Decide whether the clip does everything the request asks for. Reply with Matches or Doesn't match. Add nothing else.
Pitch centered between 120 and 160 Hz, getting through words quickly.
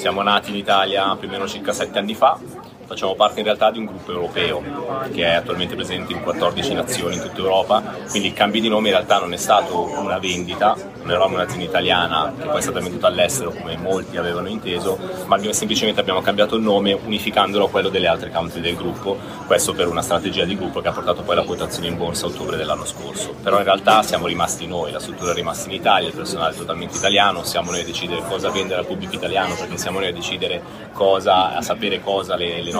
Doesn't match